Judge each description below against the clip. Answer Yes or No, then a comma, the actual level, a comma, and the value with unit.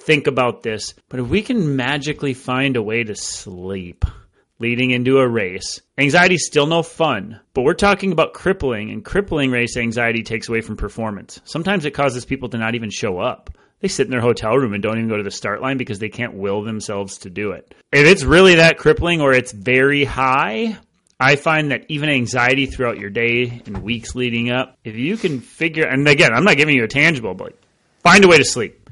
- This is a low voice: Yes, low, 125 Hz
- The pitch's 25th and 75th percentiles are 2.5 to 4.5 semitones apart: No, average, 5.0 semitones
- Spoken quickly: Yes, fast, 220 wpm